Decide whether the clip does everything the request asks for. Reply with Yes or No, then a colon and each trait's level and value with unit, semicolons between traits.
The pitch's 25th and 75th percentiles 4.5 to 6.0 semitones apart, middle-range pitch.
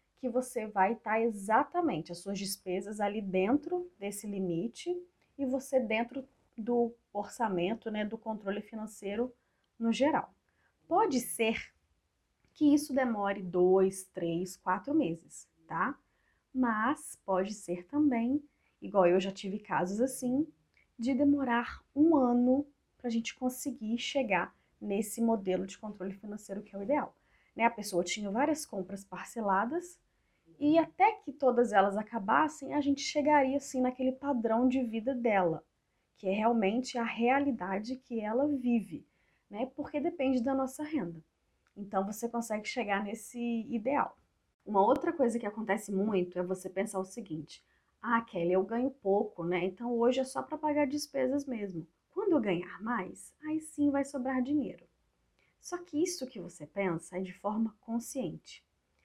No: wide, 5.5 semitones; high, 230 Hz